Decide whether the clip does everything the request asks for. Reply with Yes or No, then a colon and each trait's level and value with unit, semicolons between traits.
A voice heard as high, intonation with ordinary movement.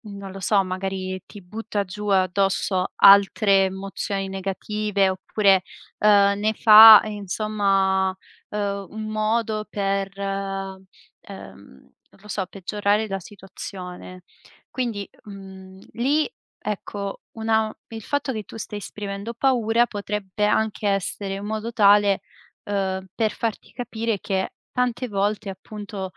No: high, 200 Hz; narrow, 1.9 semitones